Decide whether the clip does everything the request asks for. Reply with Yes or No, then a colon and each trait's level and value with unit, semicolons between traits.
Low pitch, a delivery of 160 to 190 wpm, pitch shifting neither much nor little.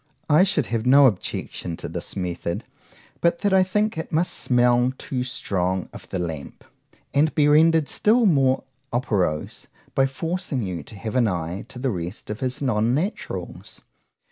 No: low, 125 Hz; average, 165 wpm; wide, 7.9 semitones